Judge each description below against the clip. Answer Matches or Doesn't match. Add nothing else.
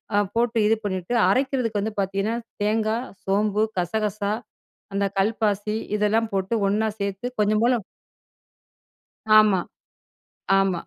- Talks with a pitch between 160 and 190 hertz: Doesn't match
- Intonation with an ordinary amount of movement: Doesn't match